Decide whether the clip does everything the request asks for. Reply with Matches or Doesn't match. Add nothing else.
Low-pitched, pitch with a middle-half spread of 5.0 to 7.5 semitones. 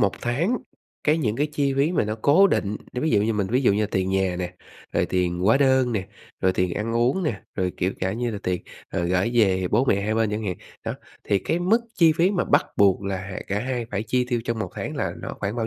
Matches